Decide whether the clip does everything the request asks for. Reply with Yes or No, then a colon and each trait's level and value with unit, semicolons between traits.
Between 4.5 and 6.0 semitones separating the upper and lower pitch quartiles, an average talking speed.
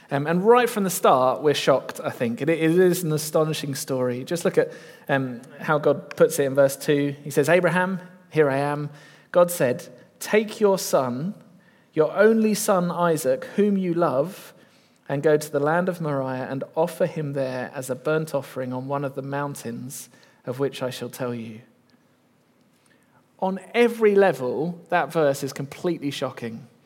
Yes: average, 4.9 semitones; average, 175 wpm